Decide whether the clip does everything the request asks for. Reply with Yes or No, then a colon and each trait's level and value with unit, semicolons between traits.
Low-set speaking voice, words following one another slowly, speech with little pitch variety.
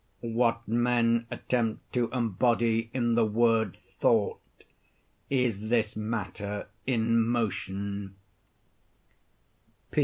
Yes: low, 115 Hz; slow, 85 wpm; narrow, 1.7 semitones